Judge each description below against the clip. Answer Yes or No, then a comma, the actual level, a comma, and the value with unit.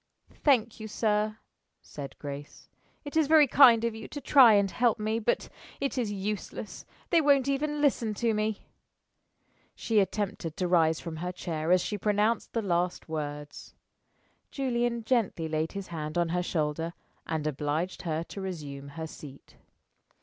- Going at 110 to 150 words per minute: No, average, 160 wpm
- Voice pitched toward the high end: Yes, high, 200 Hz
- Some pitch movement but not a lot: No, wide, 6.4 semitones